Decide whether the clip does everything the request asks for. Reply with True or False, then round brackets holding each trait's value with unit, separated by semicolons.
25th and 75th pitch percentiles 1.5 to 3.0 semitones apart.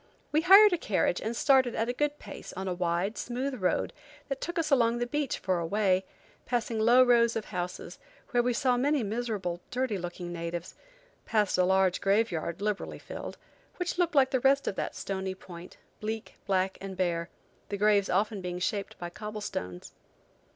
False (5.1 semitones)